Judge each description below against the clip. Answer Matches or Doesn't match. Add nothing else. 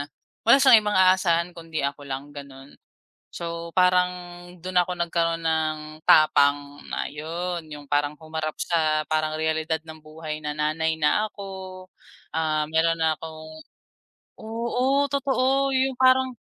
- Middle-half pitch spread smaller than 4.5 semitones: Matches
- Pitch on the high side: Doesn't match